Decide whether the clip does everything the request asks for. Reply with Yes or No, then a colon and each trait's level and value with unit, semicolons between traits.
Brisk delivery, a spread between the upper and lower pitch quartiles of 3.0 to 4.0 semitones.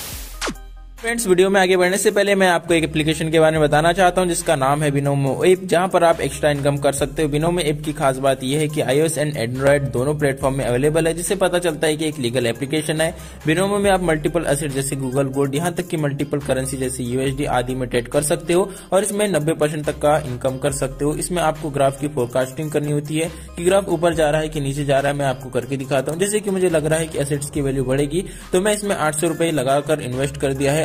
Yes: fast, 250 wpm; average, 3.6 semitones